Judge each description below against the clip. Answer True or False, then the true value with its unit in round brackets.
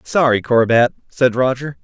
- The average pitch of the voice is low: True (120 Hz)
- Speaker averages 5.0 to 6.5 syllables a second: False (4.6 syllables/s)